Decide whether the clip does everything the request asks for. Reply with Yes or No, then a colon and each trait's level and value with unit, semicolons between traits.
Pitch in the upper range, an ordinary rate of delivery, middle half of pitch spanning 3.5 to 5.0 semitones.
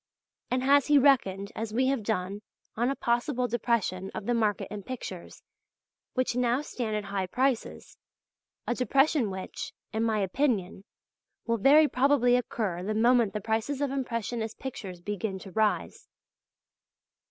Yes: high, 230 Hz; average, 150 wpm; average, 3.9 semitones